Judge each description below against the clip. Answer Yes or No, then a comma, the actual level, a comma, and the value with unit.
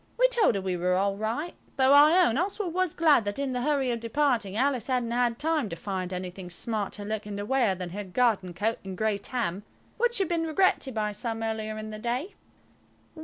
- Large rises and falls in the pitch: Yes, wide, 6.0 semitones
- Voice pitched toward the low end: No, high, 230 Hz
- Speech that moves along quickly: Yes, fast, 215 wpm